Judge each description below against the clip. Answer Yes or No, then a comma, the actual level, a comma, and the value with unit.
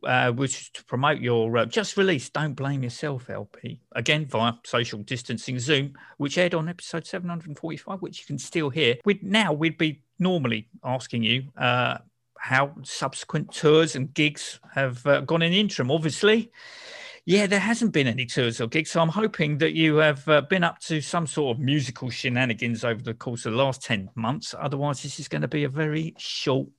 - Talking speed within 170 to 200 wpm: Yes, average, 195 wpm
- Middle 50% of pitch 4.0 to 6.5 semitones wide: Yes, average, 4.8 semitones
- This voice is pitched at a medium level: Yes, medium, 150 Hz